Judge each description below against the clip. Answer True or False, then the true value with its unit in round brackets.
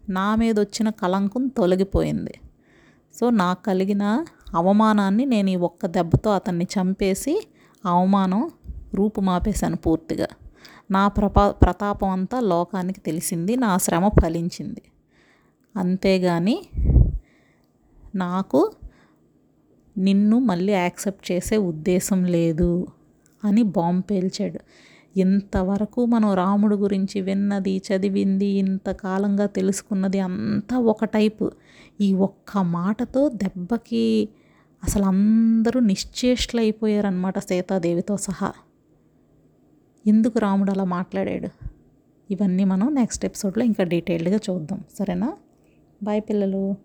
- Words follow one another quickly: False (90 wpm)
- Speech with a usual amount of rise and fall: False (2.2 semitones)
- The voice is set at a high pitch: True (195 Hz)